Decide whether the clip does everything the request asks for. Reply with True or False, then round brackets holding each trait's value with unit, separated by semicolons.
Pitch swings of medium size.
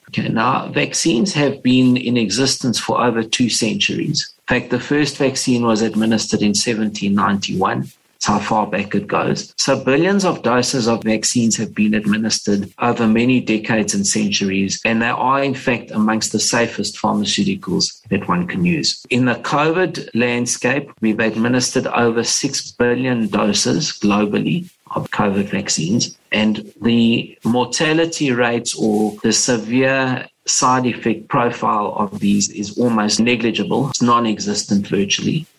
True (3.7 semitones)